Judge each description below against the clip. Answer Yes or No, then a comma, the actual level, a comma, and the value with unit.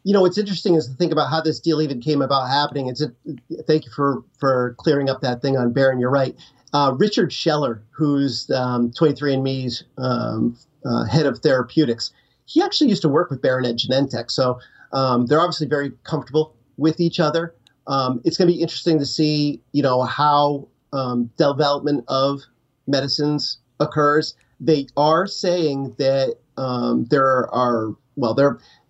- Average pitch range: Yes, average, 3.3 semitones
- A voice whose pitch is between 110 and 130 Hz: No, medium, 140 Hz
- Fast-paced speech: No, average, 170 wpm